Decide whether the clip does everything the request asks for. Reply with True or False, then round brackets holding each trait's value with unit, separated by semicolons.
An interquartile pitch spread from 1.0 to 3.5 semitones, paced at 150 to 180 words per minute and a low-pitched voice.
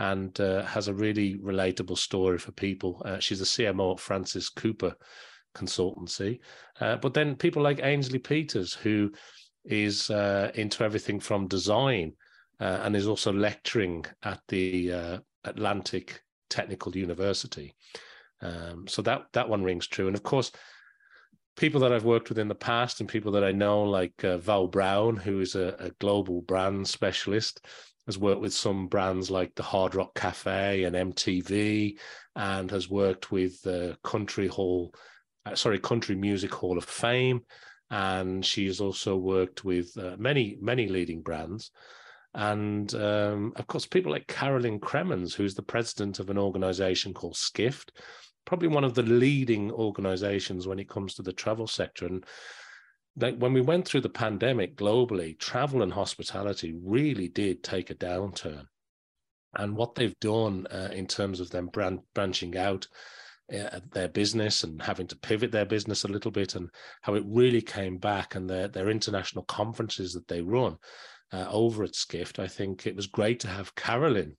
True (2.7 semitones; 170 wpm; 100 Hz)